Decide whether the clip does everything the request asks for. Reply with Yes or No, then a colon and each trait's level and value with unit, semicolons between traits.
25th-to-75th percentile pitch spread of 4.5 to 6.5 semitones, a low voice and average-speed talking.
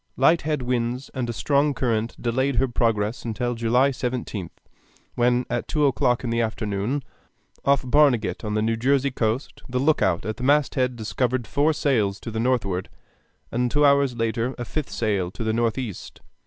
No: average, 3.2 semitones; low, 120 Hz; average, 175 wpm